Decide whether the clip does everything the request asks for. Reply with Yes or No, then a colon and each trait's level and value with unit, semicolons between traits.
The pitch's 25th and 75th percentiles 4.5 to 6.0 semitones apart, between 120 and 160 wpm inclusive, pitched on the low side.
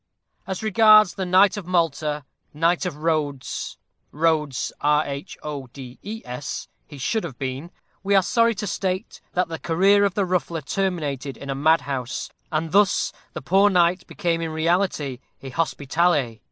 No: average, 4.8 semitones; average, 140 wpm; medium, 165 Hz